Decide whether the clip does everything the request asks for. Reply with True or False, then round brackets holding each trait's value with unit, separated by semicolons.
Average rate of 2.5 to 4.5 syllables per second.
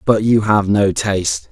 True (4.3 syllables/s)